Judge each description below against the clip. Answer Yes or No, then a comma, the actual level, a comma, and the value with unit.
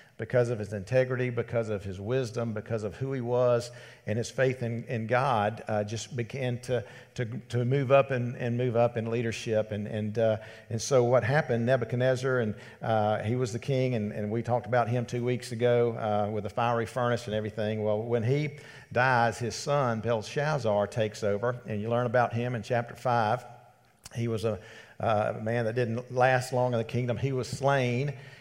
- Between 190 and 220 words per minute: Yes, average, 200 wpm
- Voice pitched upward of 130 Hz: No, low, 120 Hz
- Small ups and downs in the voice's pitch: Yes, narrow, 1.9 semitones